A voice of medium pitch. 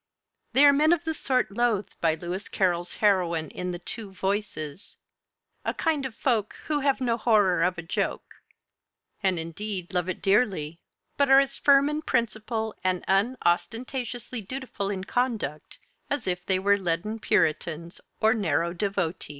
No: high, 200 Hz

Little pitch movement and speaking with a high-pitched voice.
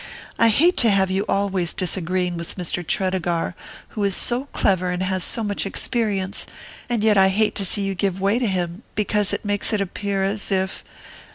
Yes: narrow, 2.0 semitones; high, 195 Hz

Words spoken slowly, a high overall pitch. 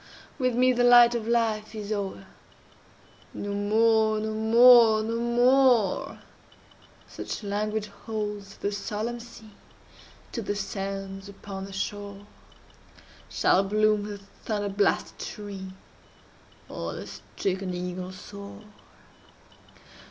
Yes: slow, 105 wpm; high, 210 Hz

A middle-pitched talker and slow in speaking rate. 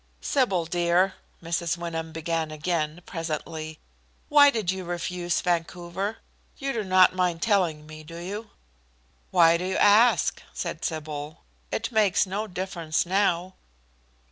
Yes: medium, 175 Hz; slow, 130 wpm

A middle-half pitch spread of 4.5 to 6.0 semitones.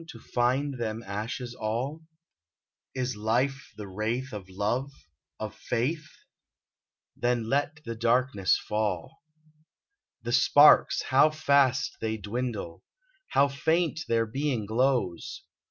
No: average, 4.0 semitones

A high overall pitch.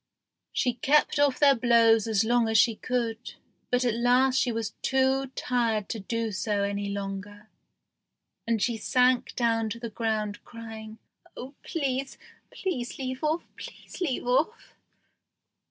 Yes: high, 235 Hz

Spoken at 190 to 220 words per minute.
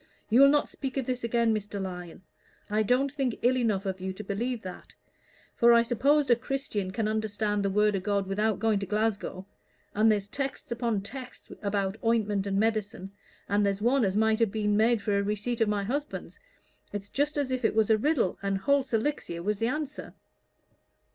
Yes: average, 195 wpm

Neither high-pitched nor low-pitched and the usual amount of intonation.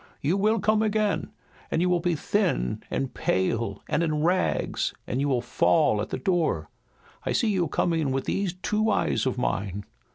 No: medium, 165 Hz; wide, 7.5 semitones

